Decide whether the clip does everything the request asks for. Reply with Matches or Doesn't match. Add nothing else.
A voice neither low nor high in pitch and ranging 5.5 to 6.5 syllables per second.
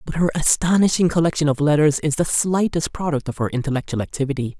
Matches